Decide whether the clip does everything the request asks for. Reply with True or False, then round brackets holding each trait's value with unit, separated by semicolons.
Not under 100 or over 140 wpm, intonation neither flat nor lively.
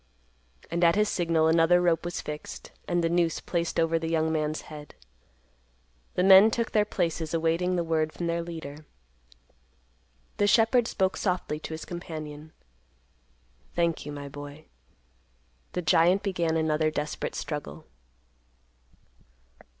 False (135 wpm; 2.1 semitones)